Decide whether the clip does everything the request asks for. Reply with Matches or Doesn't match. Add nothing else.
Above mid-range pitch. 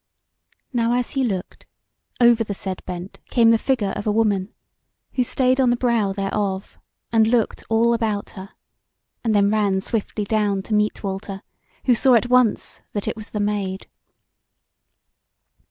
Matches